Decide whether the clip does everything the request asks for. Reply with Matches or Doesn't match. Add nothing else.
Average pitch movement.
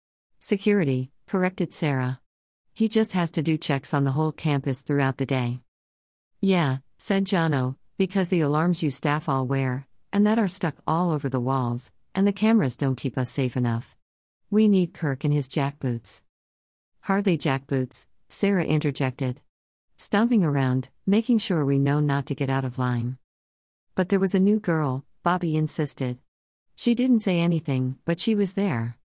Doesn't match